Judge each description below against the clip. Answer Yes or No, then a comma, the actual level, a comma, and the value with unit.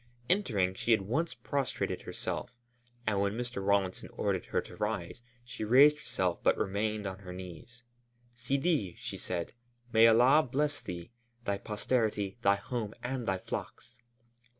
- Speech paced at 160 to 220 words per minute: No, average, 150 wpm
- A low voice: Yes, low, 110 Hz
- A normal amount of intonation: Yes, average, 4.2 semitones